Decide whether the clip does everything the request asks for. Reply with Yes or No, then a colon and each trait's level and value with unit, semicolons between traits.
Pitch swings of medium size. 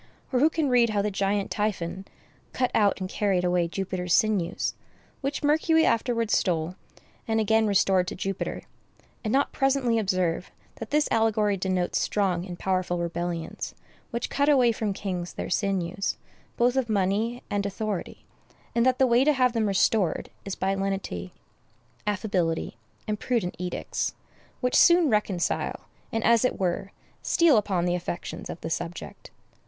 Yes: average, 4.4 semitones